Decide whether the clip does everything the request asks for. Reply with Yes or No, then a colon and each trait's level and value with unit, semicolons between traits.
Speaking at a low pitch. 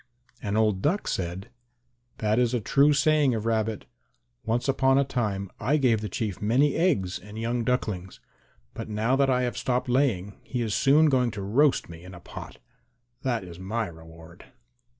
Yes: low, 115 Hz